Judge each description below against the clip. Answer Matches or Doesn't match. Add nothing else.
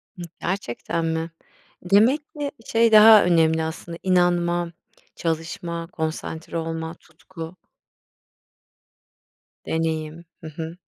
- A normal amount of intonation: Doesn't match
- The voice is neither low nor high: Matches